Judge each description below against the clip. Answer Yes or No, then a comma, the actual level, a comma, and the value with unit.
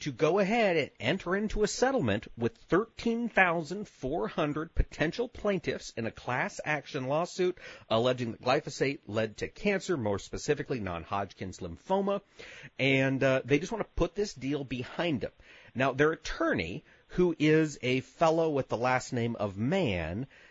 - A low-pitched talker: No, medium, 150 Hz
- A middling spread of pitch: No, wide, 6.9 semitones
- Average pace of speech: Yes, average, 150 wpm